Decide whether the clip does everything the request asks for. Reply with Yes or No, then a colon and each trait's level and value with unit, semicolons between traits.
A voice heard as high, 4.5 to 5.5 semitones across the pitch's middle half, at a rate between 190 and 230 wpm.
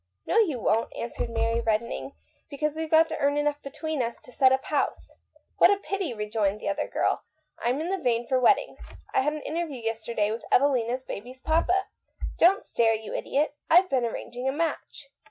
Yes: very high, 265 Hz; average, 5.2 semitones; average, 200 wpm